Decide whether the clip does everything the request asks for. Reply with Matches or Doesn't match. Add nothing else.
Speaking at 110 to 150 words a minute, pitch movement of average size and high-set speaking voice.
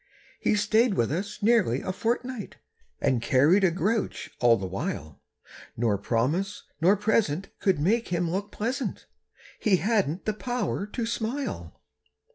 Doesn't match